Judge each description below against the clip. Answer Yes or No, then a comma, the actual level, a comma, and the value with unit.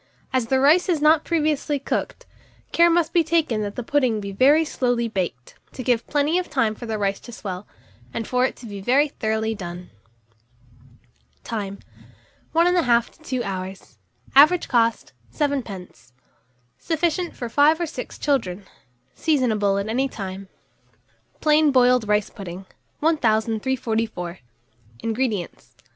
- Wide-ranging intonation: Yes, wide, 6.1 semitones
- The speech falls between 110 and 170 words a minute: Yes, average, 140 wpm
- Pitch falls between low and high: No, high, 245 Hz